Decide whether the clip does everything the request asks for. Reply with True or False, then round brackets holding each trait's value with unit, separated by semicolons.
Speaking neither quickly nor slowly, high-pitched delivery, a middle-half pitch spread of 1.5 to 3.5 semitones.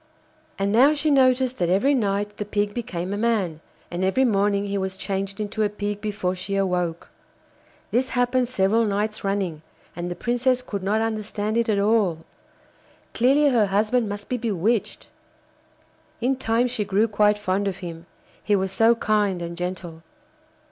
True (170 wpm; 205 Hz; 3.2 semitones)